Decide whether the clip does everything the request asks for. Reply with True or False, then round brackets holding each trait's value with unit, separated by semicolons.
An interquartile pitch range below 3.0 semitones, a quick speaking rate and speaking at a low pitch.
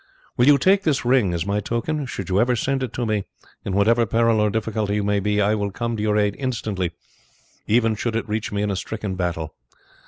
True (2.6 semitones; 230 wpm; 110 Hz)